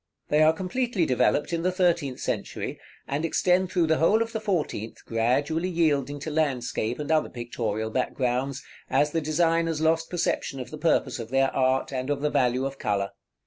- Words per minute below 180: No, average, 185 wpm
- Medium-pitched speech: Yes, medium, 150 Hz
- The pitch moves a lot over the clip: No, average, 4.5 semitones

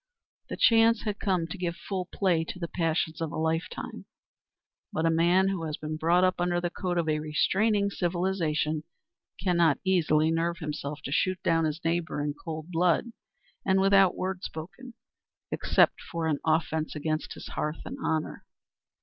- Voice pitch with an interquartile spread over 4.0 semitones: No, average, 2.9 semitones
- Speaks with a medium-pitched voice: Yes, medium, 170 Hz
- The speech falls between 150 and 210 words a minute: Yes, average, 170 wpm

